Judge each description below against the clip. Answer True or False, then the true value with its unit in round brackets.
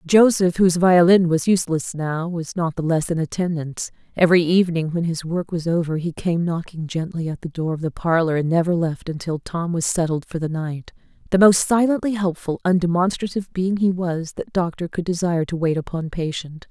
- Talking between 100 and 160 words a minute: False (200 wpm)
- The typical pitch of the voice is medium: True (170 Hz)